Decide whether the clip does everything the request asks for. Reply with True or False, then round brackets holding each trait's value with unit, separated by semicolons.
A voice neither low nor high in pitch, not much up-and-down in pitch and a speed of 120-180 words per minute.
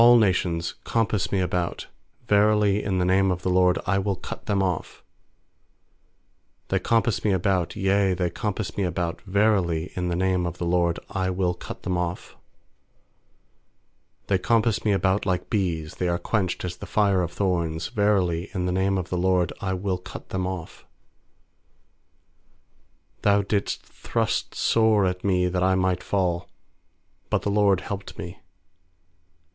False (95 Hz; 2.1 semitones; 160 wpm)